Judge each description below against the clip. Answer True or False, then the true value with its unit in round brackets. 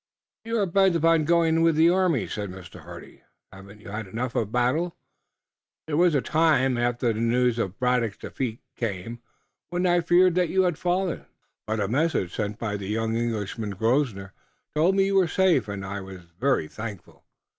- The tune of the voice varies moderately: False (7.9 semitones)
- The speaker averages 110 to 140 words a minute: False (185 wpm)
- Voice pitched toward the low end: True (125 Hz)